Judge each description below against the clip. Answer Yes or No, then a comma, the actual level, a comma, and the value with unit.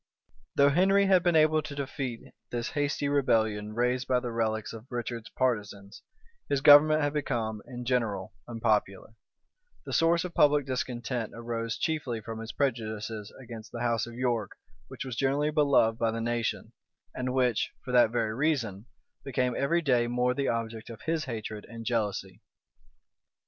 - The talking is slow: No, average, 160 wpm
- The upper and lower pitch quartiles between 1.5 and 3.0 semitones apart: No, average, 3.8 semitones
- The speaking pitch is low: Yes, low, 120 Hz